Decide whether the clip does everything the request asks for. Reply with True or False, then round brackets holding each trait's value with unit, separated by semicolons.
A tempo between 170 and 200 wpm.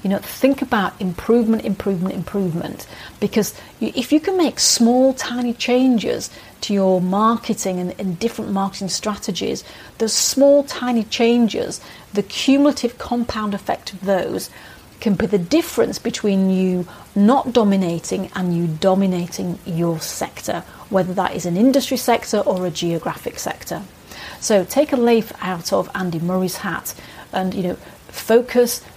False (140 wpm)